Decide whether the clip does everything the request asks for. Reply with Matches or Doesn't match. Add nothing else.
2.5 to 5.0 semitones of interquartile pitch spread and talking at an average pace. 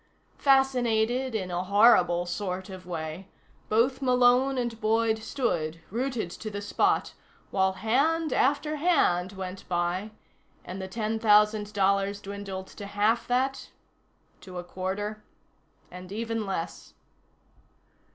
Doesn't match